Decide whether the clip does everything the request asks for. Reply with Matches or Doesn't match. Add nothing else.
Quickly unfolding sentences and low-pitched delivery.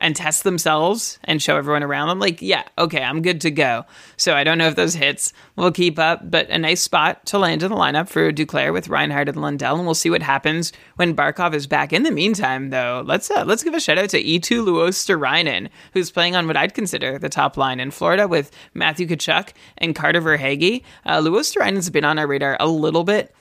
Doesn't match